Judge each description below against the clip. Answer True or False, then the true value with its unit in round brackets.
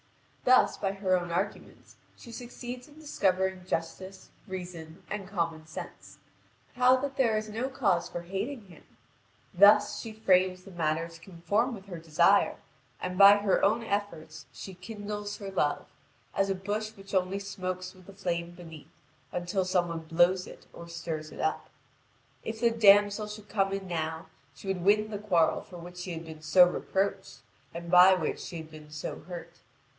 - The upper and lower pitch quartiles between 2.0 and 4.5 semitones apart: True (3.3 semitones)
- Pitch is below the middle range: False (190 Hz)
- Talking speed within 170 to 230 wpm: True (175 wpm)